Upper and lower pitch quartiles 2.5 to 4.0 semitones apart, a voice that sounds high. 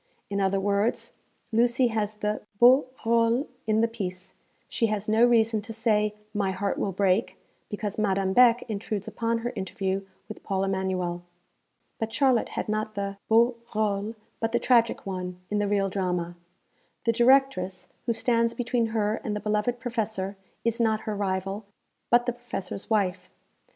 Yes: average, 2.9 semitones; high, 215 Hz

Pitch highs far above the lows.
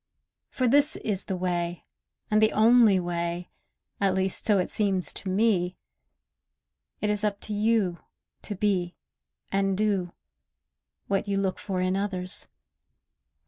No: narrow, 2.5 semitones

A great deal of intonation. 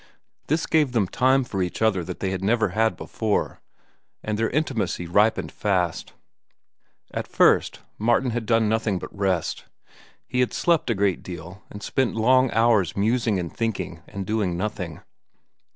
No: average, 3.8 semitones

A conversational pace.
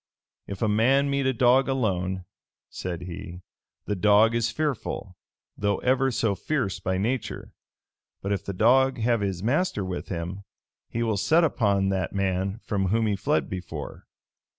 Yes: average, 165 wpm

